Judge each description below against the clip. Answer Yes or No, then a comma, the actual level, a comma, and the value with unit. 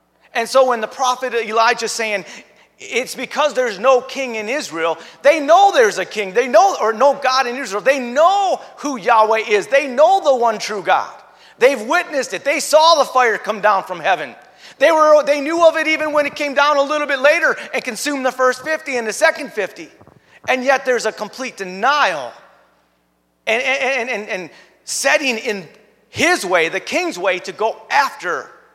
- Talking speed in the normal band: Yes, average, 190 wpm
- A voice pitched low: No, very high, 265 Hz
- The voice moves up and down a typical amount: Yes, average, 4.9 semitones